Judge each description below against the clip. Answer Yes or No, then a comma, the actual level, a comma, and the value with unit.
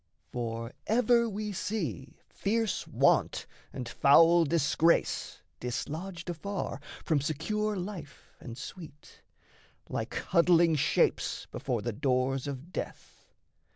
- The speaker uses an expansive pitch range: Yes, wide, 6.4 semitones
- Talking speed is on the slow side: Yes, slow, 105 wpm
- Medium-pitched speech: Yes, medium, 165 Hz